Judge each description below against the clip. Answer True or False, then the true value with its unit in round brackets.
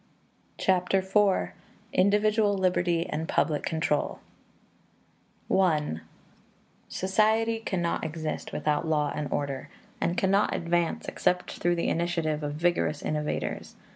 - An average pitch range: True (3.7 semitones)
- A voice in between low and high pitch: True (175 Hz)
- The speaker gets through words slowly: True (105 wpm)